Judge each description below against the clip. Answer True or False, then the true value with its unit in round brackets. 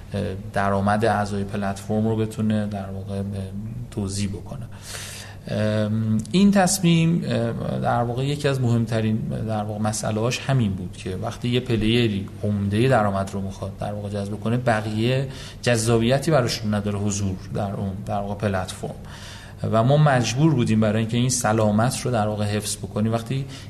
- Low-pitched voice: True (110 Hz)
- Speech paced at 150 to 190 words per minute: False (140 wpm)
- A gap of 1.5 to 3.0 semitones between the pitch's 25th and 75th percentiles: True (2.7 semitones)